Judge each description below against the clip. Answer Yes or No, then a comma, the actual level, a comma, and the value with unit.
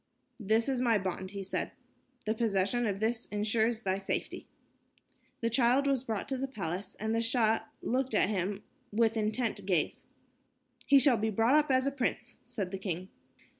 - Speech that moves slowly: No, average, 175 wpm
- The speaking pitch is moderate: No, high, 225 Hz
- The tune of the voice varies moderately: Yes, average, 3.6 semitones